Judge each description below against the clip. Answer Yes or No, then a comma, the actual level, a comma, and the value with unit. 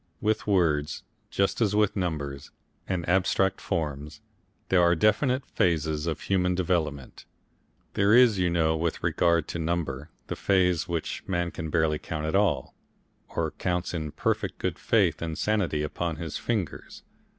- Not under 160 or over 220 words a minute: No, average, 150 wpm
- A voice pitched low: Yes, very low, 85 Hz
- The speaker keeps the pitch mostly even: No, average, 3.4 semitones